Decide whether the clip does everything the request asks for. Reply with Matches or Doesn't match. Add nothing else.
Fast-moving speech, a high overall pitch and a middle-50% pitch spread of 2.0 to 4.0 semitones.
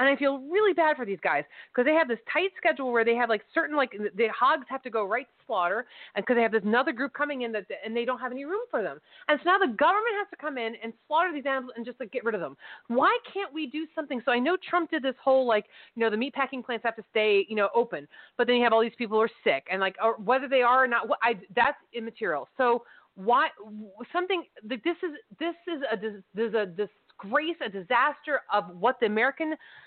Doesn't match